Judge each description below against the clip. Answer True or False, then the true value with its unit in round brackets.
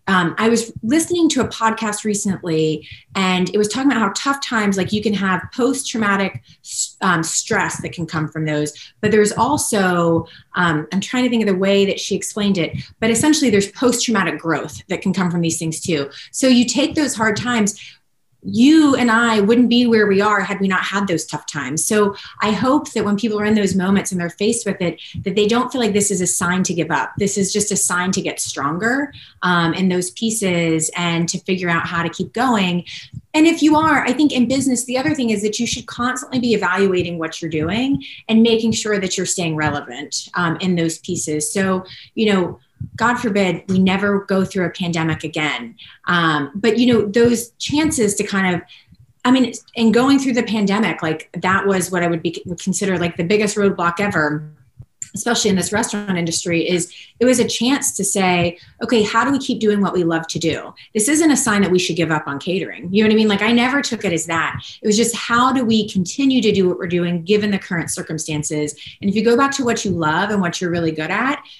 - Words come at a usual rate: False (230 wpm)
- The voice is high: True (195 Hz)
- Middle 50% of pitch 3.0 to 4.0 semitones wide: False (4.9 semitones)